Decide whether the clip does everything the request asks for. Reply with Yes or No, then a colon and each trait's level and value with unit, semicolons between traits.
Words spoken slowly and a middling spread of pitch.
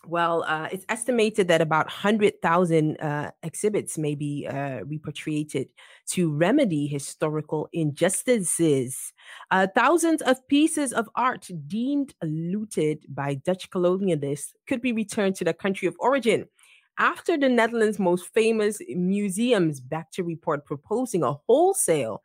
No: slow, 130 wpm; wide, 6.1 semitones